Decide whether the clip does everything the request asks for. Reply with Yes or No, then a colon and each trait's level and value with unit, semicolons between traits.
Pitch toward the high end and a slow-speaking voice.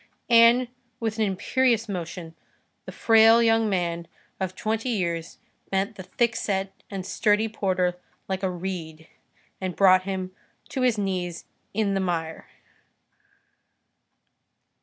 Yes: high, 195 Hz; slow, 120 wpm